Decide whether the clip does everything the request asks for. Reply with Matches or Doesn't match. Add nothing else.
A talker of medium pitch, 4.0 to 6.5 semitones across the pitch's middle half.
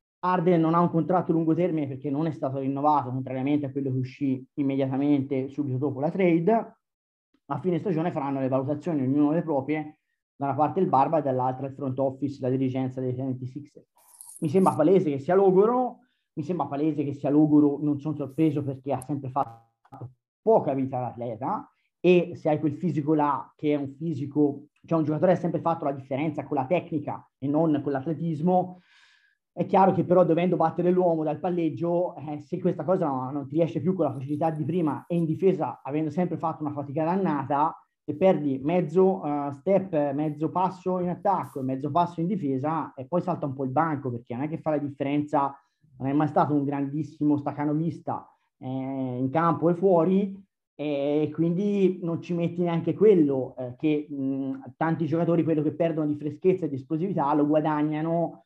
Doesn't match